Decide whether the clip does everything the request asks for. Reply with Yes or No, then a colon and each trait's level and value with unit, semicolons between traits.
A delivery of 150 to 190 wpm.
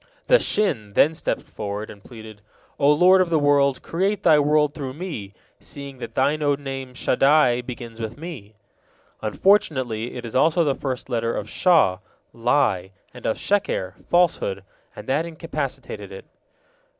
Yes: average, 155 wpm